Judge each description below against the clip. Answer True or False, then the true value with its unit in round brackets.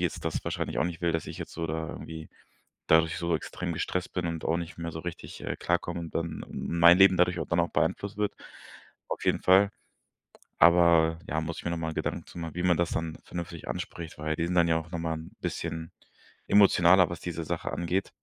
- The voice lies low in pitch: True (85 Hz)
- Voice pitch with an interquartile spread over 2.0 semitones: False (1.4 semitones)